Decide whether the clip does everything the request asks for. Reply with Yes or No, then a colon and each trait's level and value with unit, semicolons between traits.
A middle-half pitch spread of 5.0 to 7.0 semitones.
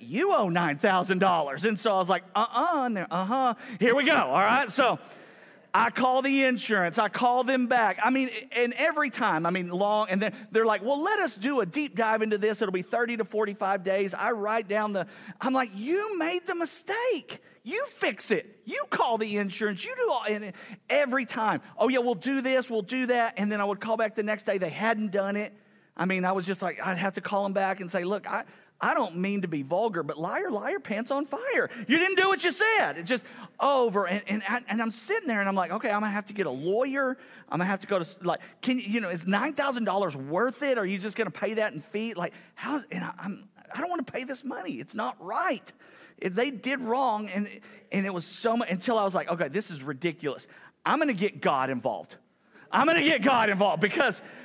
No: average, 4.6 semitones